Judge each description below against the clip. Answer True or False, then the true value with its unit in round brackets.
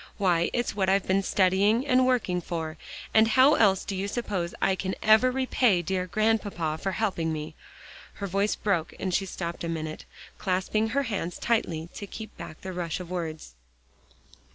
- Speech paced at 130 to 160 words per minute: False (175 wpm)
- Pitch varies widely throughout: False (4.1 semitones)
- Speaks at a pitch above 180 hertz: True (190 Hz)